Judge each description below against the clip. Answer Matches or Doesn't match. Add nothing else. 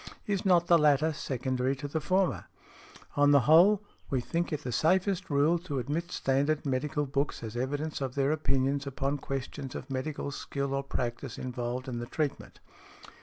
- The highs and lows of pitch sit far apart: Doesn't match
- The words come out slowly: Doesn't match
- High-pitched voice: Doesn't match